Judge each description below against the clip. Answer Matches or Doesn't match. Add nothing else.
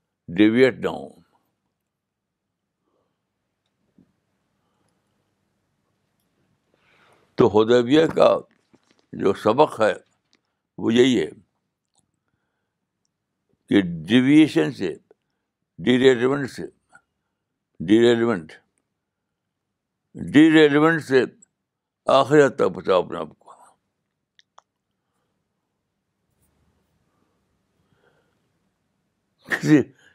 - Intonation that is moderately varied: Matches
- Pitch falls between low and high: Doesn't match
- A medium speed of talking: Doesn't match